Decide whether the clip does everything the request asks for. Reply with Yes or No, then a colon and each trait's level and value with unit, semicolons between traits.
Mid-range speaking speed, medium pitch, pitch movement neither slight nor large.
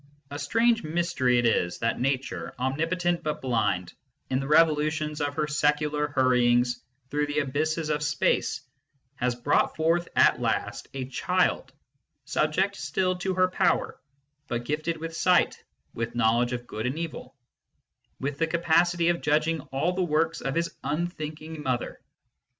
Yes: average, 150 wpm; medium, 150 Hz; average, 4.1 semitones